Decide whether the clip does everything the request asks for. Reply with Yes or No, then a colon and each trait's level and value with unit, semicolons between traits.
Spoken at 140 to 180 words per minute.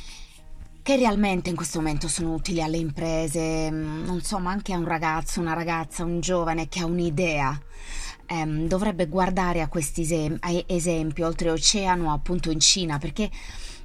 Yes: average, 160 wpm